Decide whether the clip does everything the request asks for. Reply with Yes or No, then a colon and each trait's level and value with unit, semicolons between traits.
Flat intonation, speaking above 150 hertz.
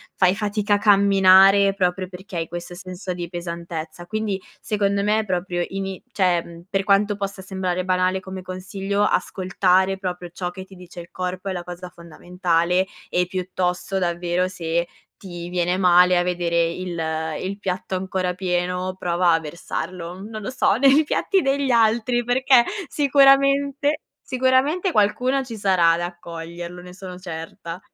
Yes: narrow, 2.3 semitones; medium, 185 Hz